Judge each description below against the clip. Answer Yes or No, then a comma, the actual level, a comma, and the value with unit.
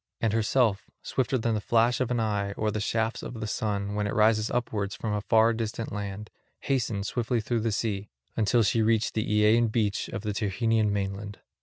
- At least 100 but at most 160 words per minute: No, average, 200 wpm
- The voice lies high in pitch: No, low, 110 Hz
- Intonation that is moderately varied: No, narrow, 1.8 semitones